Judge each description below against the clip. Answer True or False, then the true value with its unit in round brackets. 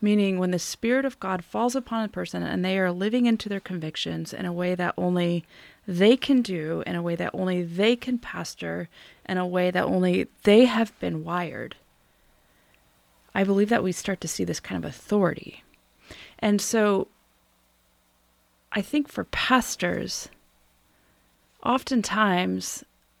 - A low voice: False (180 Hz)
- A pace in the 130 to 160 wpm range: True (155 wpm)